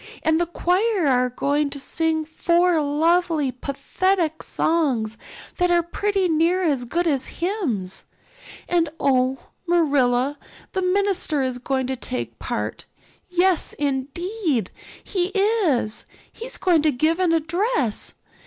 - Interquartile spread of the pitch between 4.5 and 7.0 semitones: Yes, average, 4.8 semitones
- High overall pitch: Yes, very high, 320 Hz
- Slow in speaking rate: Yes, slow, 125 wpm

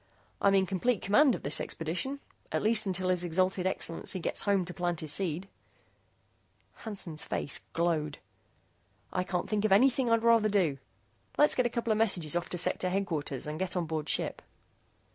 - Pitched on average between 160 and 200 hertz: Yes, medium, 185 Hz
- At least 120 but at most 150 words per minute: No, average, 180 wpm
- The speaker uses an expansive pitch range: No, average, 4.2 semitones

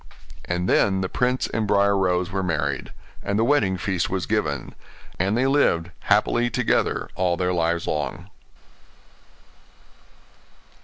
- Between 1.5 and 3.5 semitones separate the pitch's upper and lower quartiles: Yes, average, 3.1 semitones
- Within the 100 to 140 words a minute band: Yes, slow, 135 wpm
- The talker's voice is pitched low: Yes, very low, 95 Hz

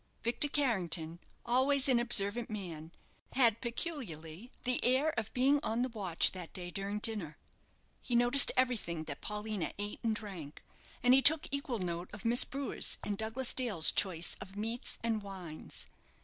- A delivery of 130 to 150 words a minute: No, average, 160 wpm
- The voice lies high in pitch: Yes, high, 220 Hz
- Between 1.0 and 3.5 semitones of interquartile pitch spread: No, average, 5.3 semitones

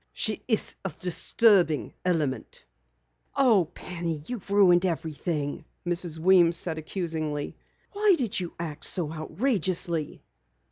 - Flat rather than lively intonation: No, average, 3.4 semitones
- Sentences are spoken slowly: Yes, slow, 110 wpm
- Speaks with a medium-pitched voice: Yes, medium, 175 Hz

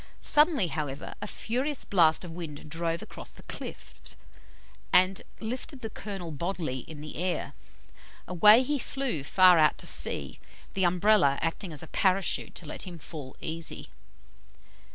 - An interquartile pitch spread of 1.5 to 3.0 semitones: No, average, 4.8 semitones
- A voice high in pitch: No, medium, 175 Hz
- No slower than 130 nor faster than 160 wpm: Yes, average, 150 wpm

